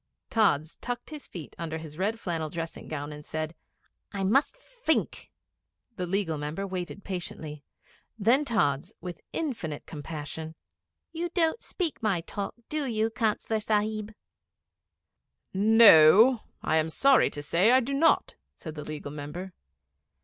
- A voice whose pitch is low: No, high, 190 Hz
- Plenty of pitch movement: Yes, wide, 6.5 semitones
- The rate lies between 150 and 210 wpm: No, average, 140 wpm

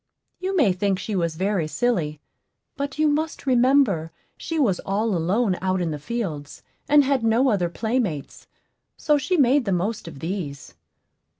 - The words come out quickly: No, average, 165 wpm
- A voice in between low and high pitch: No, high, 210 Hz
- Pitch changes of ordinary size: No, wide, 7.4 semitones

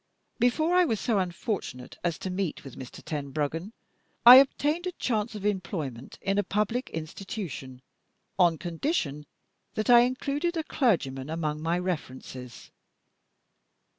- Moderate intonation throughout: No, wide, 8.0 semitones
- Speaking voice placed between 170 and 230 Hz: Yes, medium, 185 Hz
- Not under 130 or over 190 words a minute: Yes, slow, 135 wpm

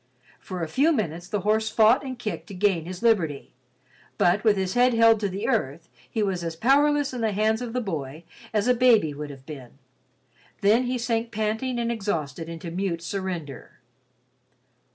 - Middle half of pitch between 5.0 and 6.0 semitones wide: Yes, wide, 5.6 semitones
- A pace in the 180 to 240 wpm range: Yes, average, 185 wpm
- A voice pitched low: No, high, 210 Hz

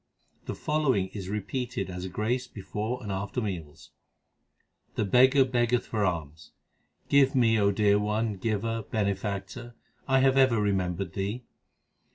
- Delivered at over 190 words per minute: No, average, 140 wpm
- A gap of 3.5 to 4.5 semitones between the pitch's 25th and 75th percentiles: Yes, average, 4.1 semitones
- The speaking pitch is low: Yes, low, 105 Hz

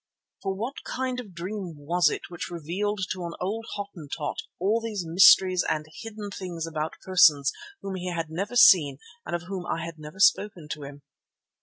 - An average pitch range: Yes, average, 3.7 semitones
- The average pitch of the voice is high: No, medium, 180 Hz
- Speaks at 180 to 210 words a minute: Yes, average, 185 wpm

